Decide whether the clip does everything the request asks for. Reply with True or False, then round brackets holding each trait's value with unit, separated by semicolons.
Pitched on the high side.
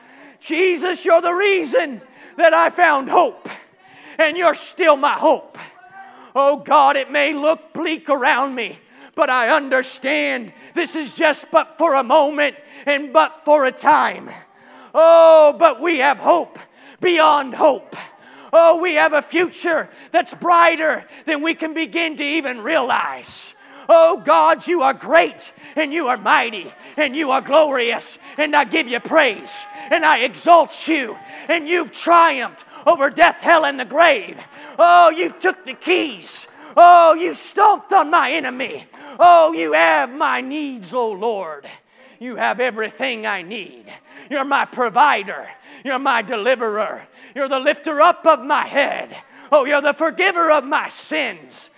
True (310 Hz)